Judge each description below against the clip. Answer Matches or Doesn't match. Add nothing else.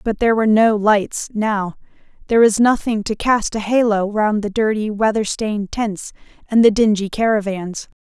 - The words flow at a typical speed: Matches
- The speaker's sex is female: Matches